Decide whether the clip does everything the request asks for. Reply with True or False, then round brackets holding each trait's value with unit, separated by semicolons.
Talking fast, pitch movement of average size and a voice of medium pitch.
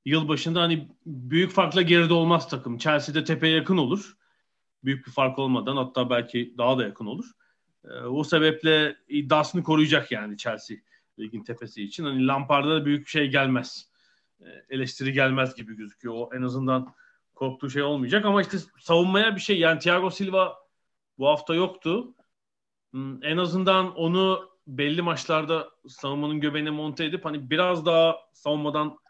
True (155 wpm; 4.3 semitones; 155 Hz)